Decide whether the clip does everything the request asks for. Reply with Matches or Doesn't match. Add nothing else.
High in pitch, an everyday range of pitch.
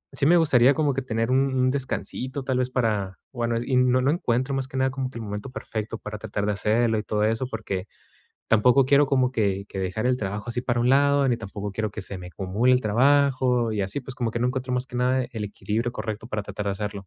Doesn't match